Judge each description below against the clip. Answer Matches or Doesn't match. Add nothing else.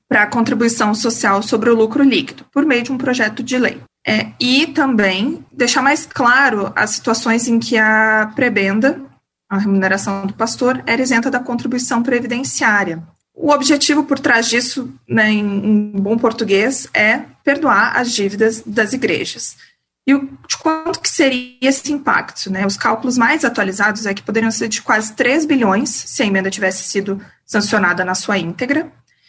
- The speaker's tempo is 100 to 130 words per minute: Doesn't match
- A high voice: Matches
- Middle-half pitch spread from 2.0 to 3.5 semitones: Doesn't match